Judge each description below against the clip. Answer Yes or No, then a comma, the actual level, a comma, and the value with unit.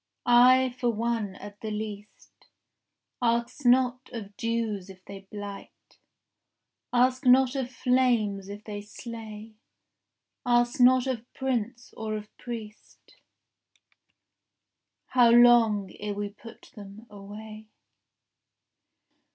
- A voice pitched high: Yes, high, 225 Hz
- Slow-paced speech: Yes, slow, 105 wpm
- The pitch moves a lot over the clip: No, average, 3.0 semitones